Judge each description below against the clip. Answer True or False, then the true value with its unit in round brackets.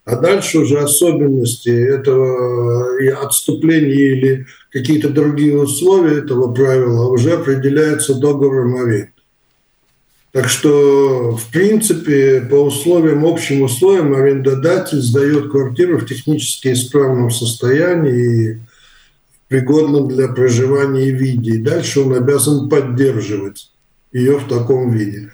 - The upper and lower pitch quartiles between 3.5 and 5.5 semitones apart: False (2.6 semitones)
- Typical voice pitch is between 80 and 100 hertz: False (135 Hz)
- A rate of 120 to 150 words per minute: False (110 wpm)